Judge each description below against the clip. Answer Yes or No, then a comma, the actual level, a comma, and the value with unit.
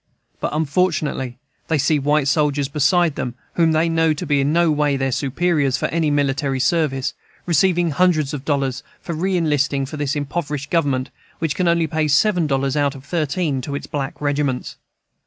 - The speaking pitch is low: No, medium, 150 Hz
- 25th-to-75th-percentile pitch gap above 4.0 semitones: No, average, 2.9 semitones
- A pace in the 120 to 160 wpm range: No, average, 180 wpm